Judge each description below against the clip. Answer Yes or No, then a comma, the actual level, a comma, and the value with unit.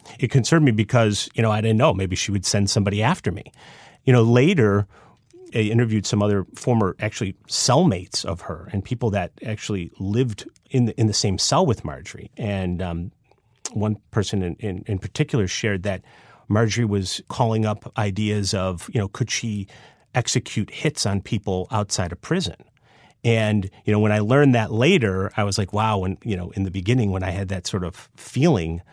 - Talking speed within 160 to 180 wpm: No, average, 195 wpm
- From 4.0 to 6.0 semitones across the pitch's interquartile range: No, average, 3.3 semitones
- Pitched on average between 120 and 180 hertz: No, low, 105 Hz